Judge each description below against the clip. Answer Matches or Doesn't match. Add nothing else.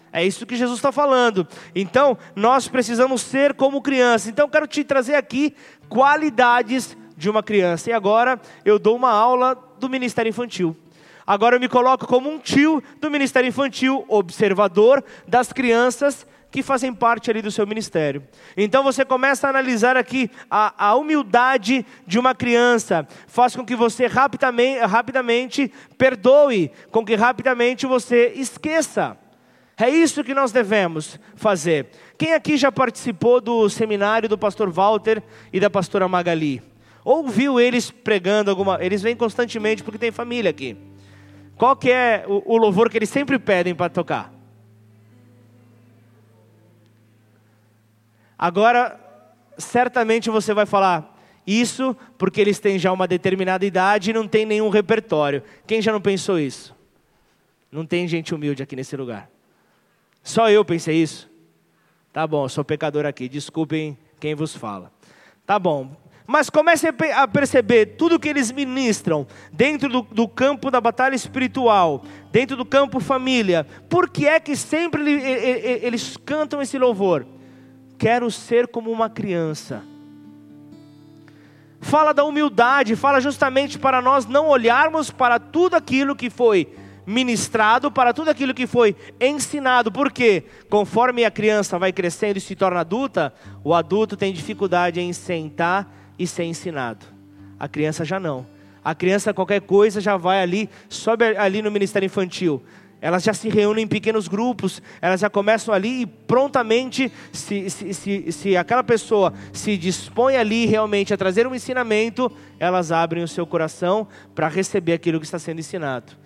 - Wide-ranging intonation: Matches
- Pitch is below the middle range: Doesn't match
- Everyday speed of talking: Matches